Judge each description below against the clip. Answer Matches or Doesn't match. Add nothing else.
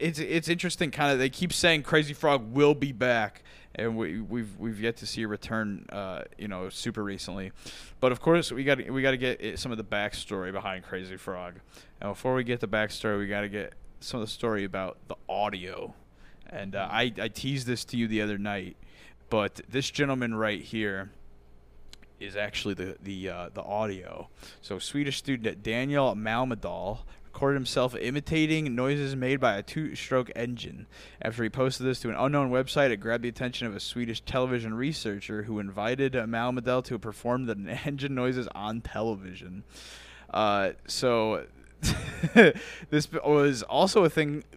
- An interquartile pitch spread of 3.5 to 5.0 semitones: Matches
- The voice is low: Matches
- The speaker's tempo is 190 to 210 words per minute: Doesn't match